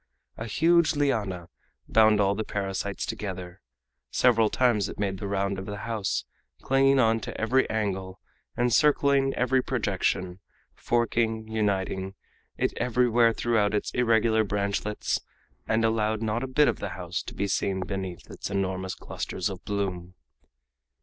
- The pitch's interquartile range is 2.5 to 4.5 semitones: Yes, average, 3.3 semitones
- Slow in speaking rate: No, average, 145 wpm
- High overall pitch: No, low, 105 Hz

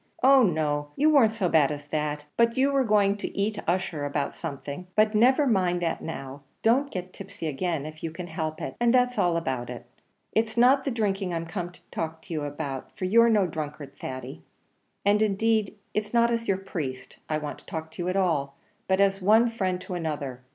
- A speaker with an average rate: No, fast, 215 wpm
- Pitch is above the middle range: No, medium, 180 Hz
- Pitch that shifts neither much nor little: No, wide, 6.0 semitones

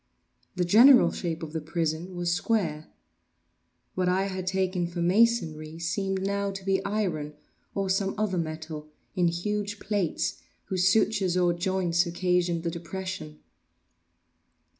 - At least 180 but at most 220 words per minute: No, slow, 135 wpm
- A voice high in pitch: No, medium, 180 Hz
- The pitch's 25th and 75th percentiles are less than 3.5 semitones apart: Yes, narrow, 2.6 semitones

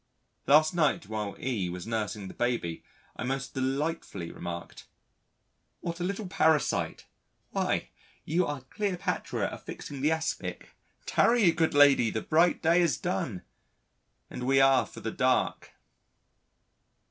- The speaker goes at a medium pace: No, slow, 130 wpm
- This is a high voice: No, low, 135 Hz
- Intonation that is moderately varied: No, wide, 6.6 semitones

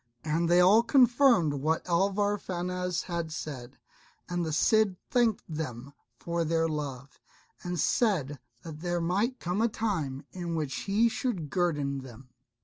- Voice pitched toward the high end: No, medium, 170 Hz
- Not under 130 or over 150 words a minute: Yes, average, 145 wpm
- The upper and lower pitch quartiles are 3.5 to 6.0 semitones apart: Yes, average, 4.8 semitones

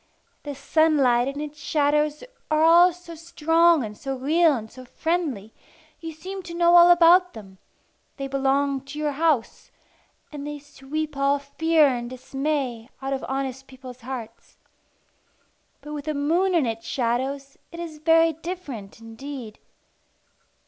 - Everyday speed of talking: Yes, average, 150 wpm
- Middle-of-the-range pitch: No, very high, 285 Hz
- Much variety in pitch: No, average, 3.7 semitones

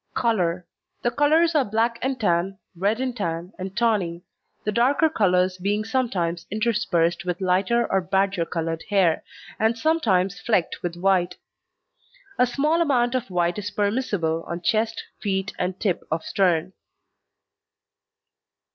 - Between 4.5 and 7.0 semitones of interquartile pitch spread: Yes, average, 4.8 semitones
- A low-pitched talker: No, high, 195 Hz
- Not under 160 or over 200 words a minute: No, average, 140 wpm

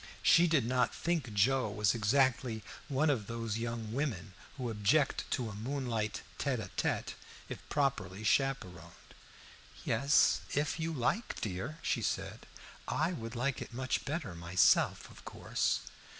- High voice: No, low, 120 Hz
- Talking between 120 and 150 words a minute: Yes, average, 145 wpm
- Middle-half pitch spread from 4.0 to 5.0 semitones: Yes, average, 4.7 semitones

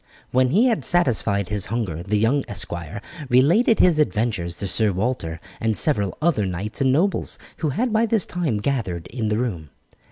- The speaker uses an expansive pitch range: Yes, wide, 7.3 semitones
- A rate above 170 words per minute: Yes, average, 180 wpm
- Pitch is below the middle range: Yes, low, 115 Hz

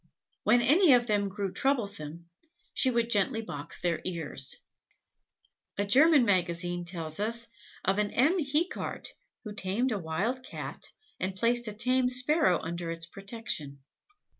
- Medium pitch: No, high, 205 Hz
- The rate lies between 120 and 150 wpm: Yes, average, 140 wpm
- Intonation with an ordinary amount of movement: No, wide, 6.0 semitones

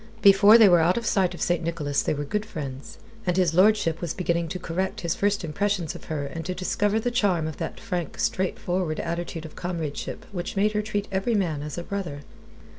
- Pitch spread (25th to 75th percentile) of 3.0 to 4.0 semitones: Yes, average, 3.7 semitones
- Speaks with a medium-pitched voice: Yes, medium, 180 Hz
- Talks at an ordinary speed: No, fast, 215 wpm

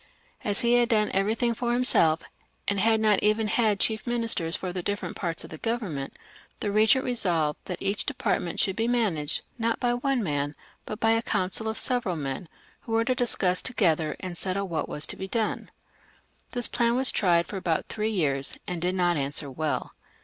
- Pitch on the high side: Yes, high, 205 Hz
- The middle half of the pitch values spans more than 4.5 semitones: Yes, average, 5.1 semitones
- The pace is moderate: No, fast, 210 wpm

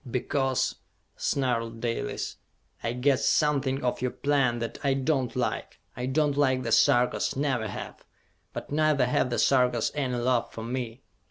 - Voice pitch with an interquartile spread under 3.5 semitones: Yes, narrow, 2.4 semitones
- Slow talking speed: No, average, 165 wpm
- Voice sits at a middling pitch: No, low, 130 Hz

